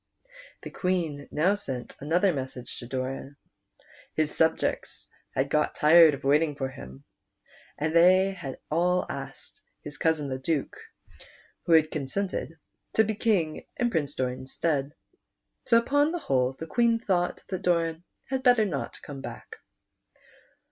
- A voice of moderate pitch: Yes, medium, 160 Hz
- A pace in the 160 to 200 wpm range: No, average, 145 wpm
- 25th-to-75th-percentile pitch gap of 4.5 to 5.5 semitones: Yes, average, 5.2 semitones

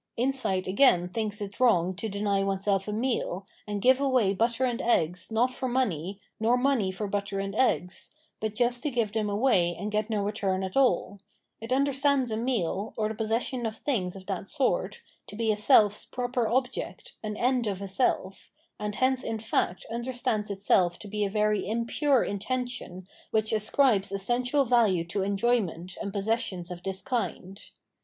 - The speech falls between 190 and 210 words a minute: No, average, 180 wpm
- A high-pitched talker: Yes, high, 215 Hz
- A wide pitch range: No, average, 3.9 semitones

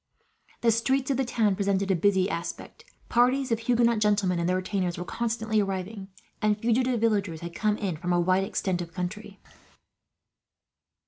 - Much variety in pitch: No, average, 3.8 semitones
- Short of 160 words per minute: No, average, 170 wpm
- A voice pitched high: Yes, high, 205 Hz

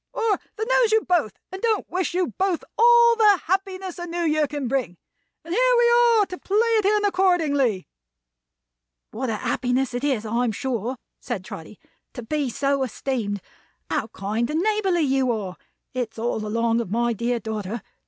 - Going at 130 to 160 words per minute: No, average, 175 wpm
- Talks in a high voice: Yes, very high, 285 Hz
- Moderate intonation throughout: No, wide, 8.8 semitones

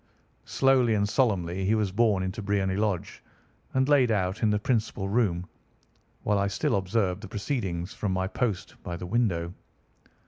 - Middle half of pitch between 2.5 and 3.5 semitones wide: Yes, average, 3.2 semitones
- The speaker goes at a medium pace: Yes, average, 165 wpm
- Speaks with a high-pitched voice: No, low, 100 Hz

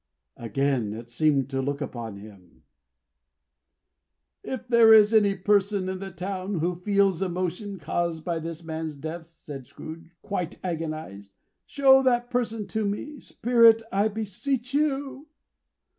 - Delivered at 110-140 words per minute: Yes, slow, 135 wpm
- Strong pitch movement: Yes, wide, 6.0 semitones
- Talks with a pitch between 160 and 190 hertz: Yes, medium, 185 Hz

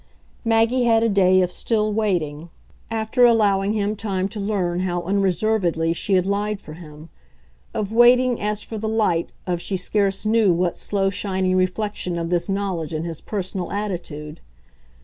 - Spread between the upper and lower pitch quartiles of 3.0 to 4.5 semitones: Yes, average, 3.3 semitones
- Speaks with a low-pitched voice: No, high, 195 Hz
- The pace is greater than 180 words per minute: No, average, 165 wpm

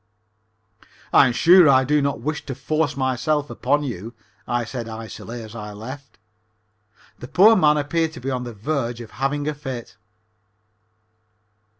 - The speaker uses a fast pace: No, average, 160 wpm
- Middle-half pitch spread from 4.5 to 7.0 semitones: No, average, 3.9 semitones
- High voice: No, low, 135 Hz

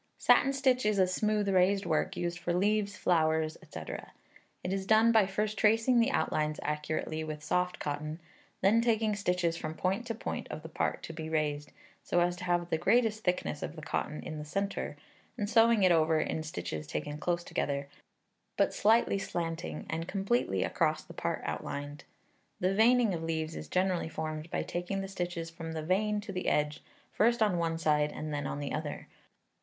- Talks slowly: No, average, 190 wpm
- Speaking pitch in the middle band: Yes, medium, 175 Hz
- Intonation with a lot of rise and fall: No, average, 4.8 semitones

